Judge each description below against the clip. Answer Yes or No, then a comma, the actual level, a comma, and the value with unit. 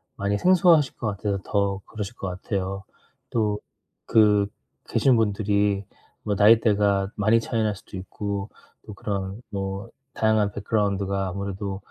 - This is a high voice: No, low, 100 Hz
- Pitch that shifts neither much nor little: No, narrow, 1.6 semitones